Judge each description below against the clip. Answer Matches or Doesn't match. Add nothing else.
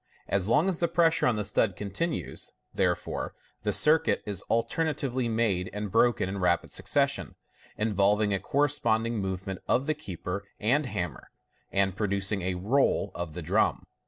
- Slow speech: Doesn't match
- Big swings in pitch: Matches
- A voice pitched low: Matches